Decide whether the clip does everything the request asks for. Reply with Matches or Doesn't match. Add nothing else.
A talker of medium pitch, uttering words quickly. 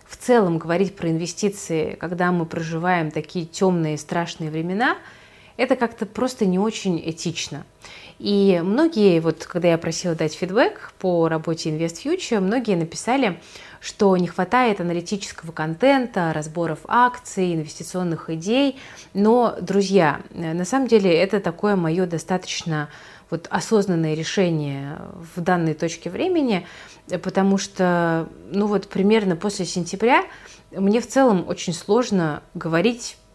Doesn't match